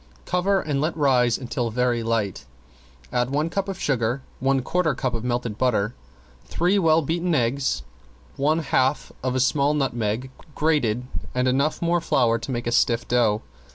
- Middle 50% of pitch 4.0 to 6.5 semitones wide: Yes, average, 4.4 semitones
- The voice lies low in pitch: Yes, low, 130 Hz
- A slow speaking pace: No, average, 165 wpm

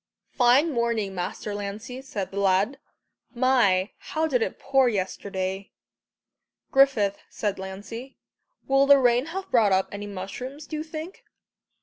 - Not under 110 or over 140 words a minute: Yes, slow, 135 wpm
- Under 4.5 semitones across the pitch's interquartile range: No, average, 5.3 semitones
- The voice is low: No, high, 235 Hz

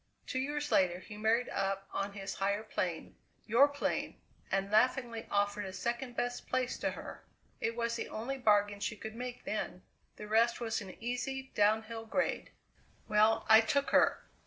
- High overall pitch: Yes, high, 225 Hz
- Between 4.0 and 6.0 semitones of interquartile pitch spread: No, average, 3.1 semitones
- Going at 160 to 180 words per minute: Yes, average, 170 wpm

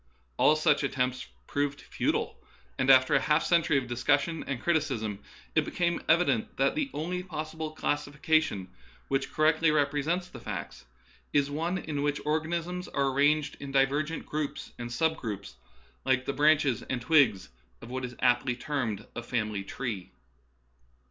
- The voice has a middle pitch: Yes, medium, 145 Hz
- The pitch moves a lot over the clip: No, average, 3.6 semitones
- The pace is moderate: Yes, average, 155 wpm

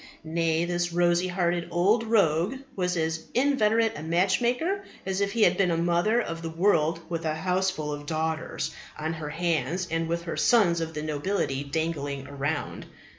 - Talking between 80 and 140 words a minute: No, average, 175 wpm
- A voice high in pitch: No, medium, 170 Hz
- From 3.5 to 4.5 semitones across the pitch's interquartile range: No, average, 3.0 semitones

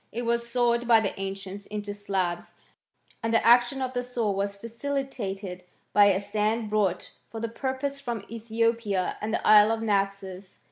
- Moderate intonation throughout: Yes, average, 3.0 semitones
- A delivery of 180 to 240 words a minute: No, average, 170 wpm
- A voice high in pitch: Yes, high, 220 Hz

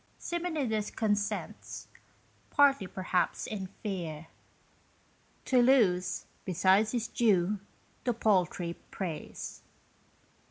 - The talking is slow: Yes, slow, 80 wpm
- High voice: Yes, high, 205 Hz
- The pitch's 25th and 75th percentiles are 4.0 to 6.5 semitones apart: Yes, average, 4.7 semitones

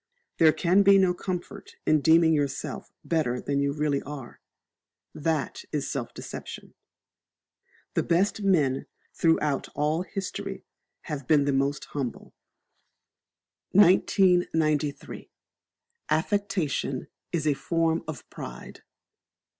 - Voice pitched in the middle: Yes, medium, 155 Hz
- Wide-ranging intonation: No, average, 3.9 semitones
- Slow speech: Yes, slow, 105 wpm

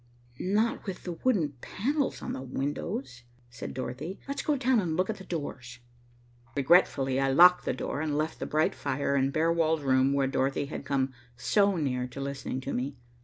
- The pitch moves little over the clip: No, average, 5.1 semitones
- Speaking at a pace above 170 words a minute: Yes, average, 190 wpm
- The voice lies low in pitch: No, medium, 145 Hz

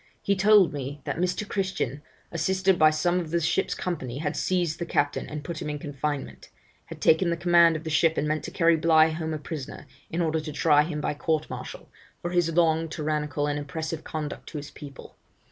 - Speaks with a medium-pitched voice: Yes, medium, 160 Hz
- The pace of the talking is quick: Yes, fast, 215 wpm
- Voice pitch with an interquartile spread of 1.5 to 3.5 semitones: Yes, narrow, 2.4 semitones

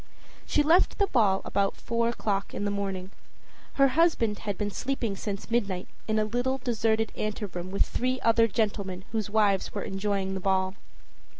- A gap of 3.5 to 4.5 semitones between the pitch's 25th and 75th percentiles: No, average, 3.0 semitones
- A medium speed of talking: Yes, average, 170 wpm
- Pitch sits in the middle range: No, high, 210 Hz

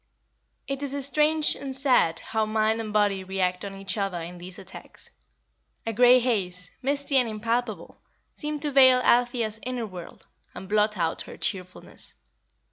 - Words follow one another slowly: No, average, 155 wpm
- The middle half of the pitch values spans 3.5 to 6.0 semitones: Yes, average, 5.2 semitones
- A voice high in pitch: Yes, high, 220 Hz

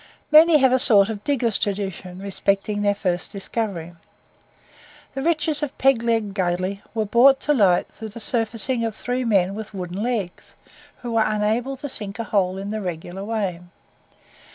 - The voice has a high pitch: Yes, high, 215 Hz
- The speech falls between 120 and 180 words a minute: Yes, average, 170 wpm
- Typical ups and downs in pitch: Yes, average, 3.7 semitones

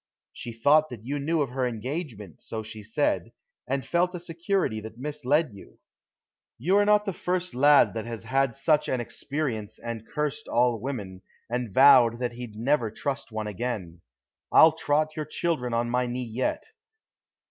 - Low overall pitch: Yes, low, 125 Hz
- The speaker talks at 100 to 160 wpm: No, average, 170 wpm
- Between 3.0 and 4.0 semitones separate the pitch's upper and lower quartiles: No, average, 4.7 semitones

